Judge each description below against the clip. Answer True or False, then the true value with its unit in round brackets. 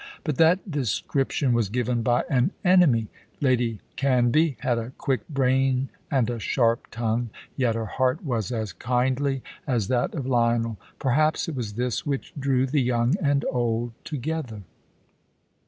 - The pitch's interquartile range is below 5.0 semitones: True (2.8 semitones)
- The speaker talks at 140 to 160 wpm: True (150 wpm)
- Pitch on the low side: True (125 Hz)